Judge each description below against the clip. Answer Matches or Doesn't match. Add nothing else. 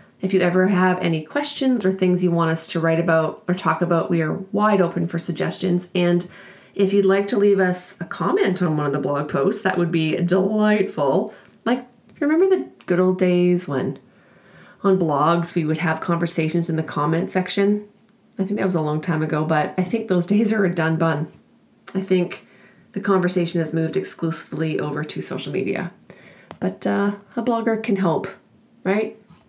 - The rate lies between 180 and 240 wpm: Matches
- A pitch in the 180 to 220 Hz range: Matches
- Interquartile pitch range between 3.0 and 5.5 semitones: Matches